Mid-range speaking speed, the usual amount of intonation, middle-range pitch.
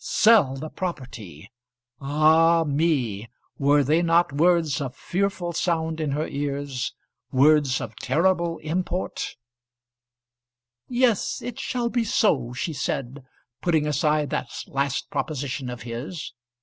No: slow, 120 wpm; average, 4.0 semitones; medium, 150 Hz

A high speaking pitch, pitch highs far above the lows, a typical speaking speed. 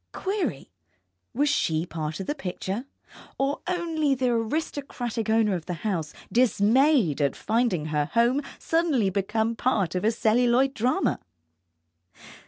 No: high, 230 Hz; wide, 6.3 semitones; slow, 130 wpm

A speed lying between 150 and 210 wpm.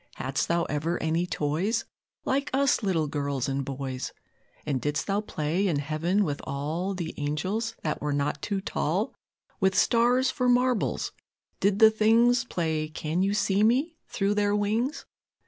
Yes: average, 160 wpm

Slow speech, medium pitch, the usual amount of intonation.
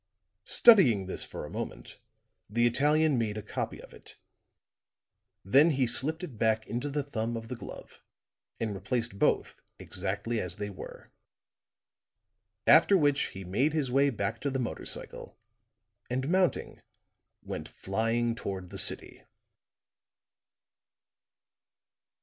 No: slow, 130 wpm; low, 120 Hz; average, 5.0 semitones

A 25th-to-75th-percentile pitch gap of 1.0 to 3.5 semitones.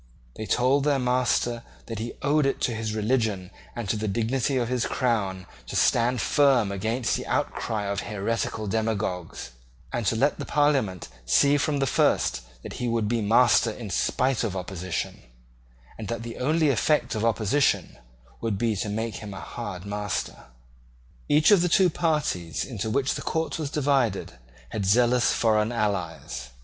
No: average, 4.2 semitones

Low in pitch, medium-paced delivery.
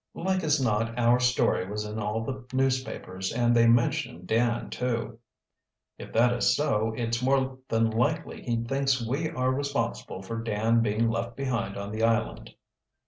Yes: low, 115 Hz; average, 165 wpm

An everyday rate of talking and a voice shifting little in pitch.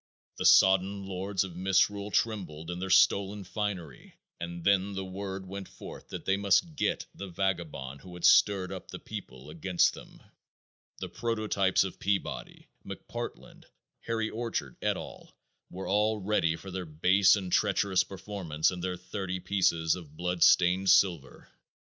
Yes: average, 155 wpm; narrow, 2.2 semitones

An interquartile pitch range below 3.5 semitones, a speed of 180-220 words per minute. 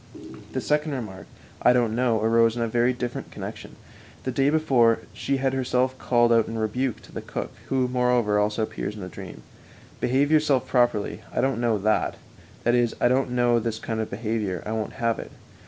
Yes: narrow, 2.4 semitones; fast, 205 wpm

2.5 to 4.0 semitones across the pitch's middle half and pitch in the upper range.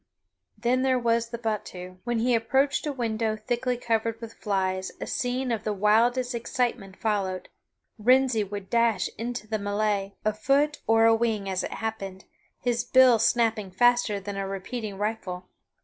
Yes: average, 3.1 semitones; high, 225 Hz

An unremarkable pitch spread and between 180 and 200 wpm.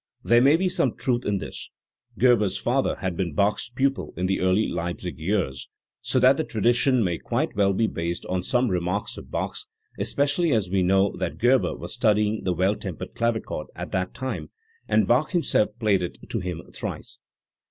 Yes: average, 5.0 semitones; average, 190 wpm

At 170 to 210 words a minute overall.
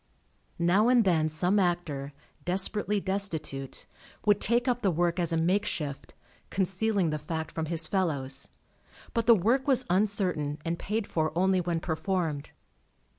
No: average, 145 wpm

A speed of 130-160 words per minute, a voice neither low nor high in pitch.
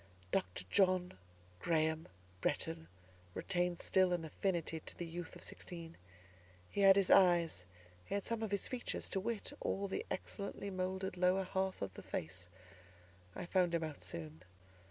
Yes: average, 155 wpm; medium, 180 Hz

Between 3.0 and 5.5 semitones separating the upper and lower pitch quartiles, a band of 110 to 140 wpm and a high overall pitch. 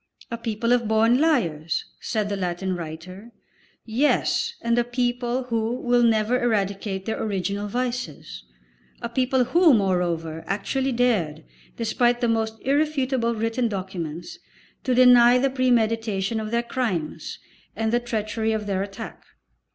Yes: average, 3.7 semitones; slow, 135 wpm; high, 225 Hz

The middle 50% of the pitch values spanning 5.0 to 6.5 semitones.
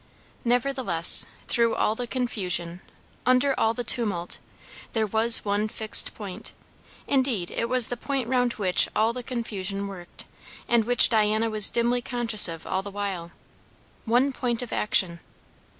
No: average, 3.6 semitones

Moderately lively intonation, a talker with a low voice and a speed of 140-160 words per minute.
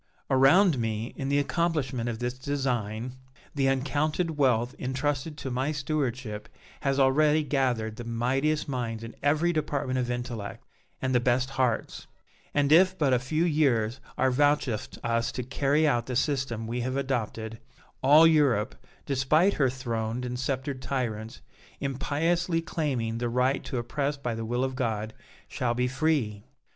Yes: average, 3.4 semitones; low, 130 Hz; average, 155 wpm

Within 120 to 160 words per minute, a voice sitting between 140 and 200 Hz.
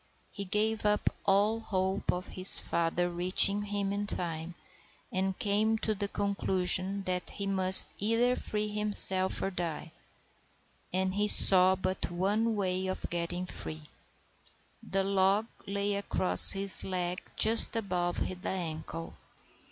Yes: slow, 135 wpm; high, 190 Hz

